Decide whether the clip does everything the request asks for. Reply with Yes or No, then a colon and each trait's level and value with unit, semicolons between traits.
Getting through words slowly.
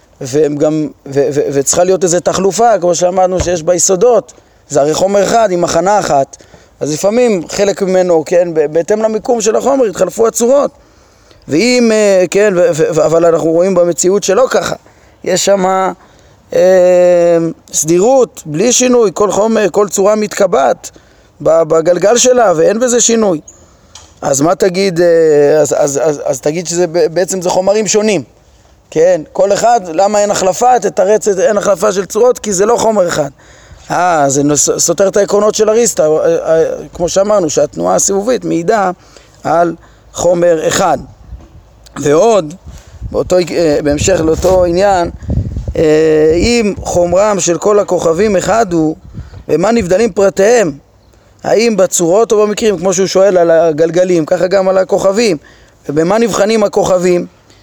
No: average, 145 wpm